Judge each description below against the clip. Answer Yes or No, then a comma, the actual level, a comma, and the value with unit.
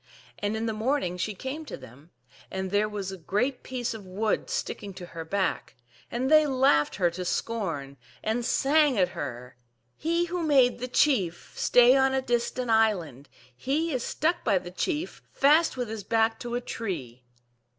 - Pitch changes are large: Yes, wide, 6.4 semitones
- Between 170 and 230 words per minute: Yes, average, 180 wpm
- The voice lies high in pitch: Yes, high, 225 Hz